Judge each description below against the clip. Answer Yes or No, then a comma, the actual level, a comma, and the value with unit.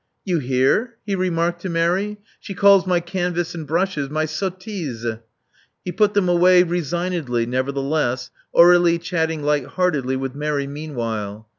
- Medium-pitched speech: Yes, medium, 165 Hz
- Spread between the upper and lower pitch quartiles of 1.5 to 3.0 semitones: No, average, 4.6 semitones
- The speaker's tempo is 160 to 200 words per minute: No, average, 150 wpm